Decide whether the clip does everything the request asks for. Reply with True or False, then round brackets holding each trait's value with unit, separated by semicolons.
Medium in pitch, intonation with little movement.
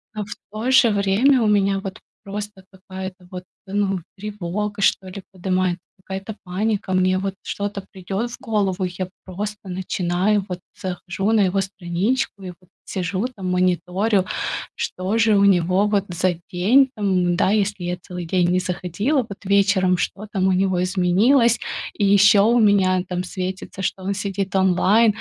False (195 Hz; 2.1 semitones)